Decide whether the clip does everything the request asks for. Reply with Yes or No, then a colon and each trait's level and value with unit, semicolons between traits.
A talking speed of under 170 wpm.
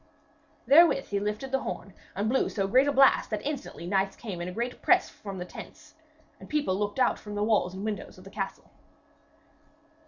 No: fast, 205 wpm